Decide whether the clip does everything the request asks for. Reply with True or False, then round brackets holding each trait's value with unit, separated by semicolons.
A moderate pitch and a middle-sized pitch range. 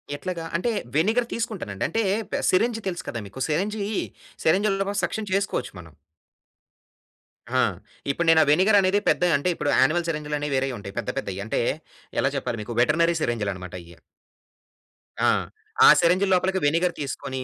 False (165 Hz; 6.7 semitones)